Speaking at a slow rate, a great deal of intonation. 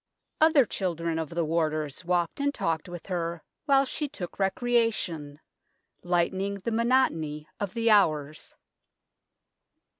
Yes: slow, 120 wpm; wide, 6.0 semitones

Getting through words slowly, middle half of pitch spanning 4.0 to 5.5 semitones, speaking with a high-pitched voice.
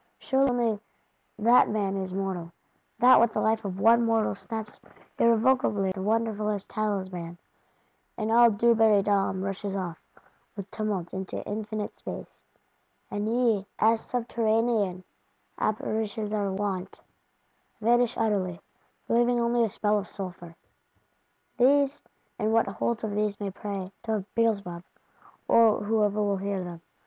No: slow, 125 wpm; average, 2.7 semitones; high, 210 Hz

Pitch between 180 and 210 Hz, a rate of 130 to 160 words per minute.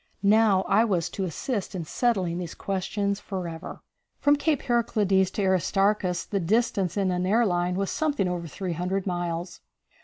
Yes: high, 190 Hz; average, 155 wpm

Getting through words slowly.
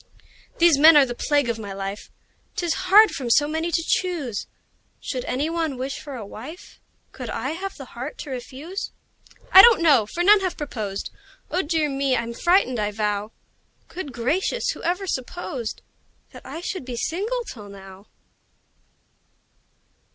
No: average, 165 wpm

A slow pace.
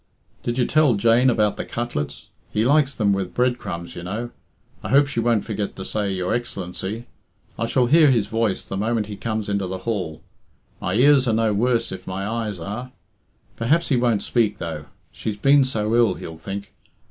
No: average, 195 wpm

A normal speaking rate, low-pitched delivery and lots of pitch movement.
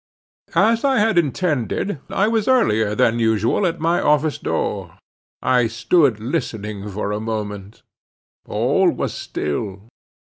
No: slow, 130 wpm; low, 120 Hz; wide, 8.6 semitones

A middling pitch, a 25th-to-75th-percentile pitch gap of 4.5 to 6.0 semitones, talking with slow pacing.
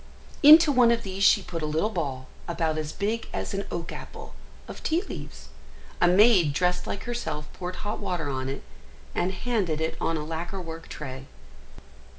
No: medium, 175 Hz; average, 5.1 semitones; average, 180 wpm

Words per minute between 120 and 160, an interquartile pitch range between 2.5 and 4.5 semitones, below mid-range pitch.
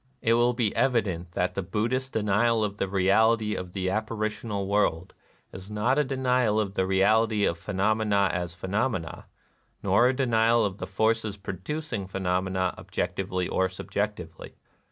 Yes: average, 155 wpm; average, 3.3 semitones; low, 105 Hz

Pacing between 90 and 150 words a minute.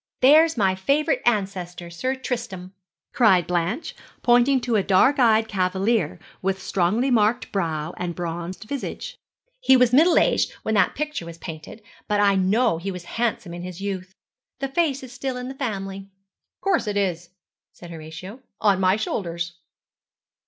No: average, 160 wpm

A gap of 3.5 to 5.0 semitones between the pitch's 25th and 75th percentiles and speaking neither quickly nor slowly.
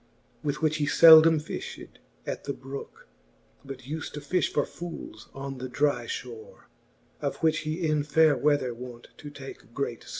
No: average, 2.7 semitones; average, 170 wpm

